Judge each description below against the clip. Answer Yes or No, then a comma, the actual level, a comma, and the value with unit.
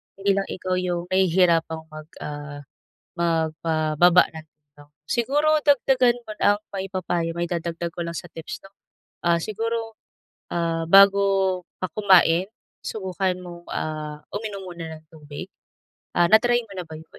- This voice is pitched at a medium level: Yes, medium, 175 Hz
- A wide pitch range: No, average, 3.4 semitones